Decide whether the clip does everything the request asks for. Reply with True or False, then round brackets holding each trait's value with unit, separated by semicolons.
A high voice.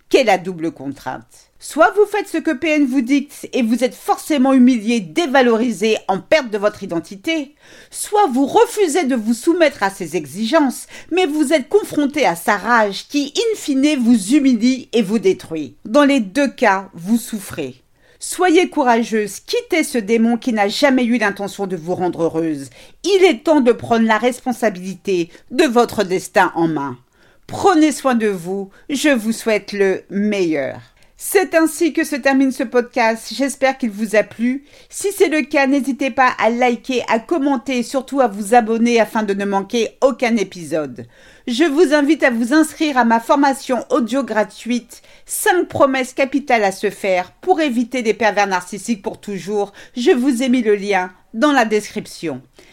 True (245 Hz)